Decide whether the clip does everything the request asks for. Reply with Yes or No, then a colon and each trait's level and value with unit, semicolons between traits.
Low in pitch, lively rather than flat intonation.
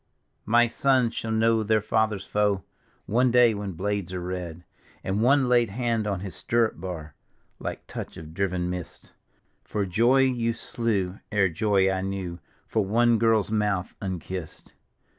No: low, 105 Hz; average, 3.6 semitones